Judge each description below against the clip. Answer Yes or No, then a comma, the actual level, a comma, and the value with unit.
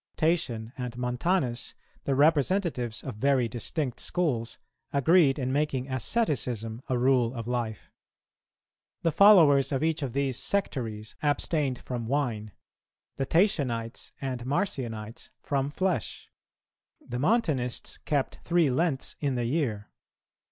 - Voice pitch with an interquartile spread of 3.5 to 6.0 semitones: Yes, average, 4.3 semitones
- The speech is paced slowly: Yes, slow, 120 wpm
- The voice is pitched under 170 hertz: Yes, low, 135 Hz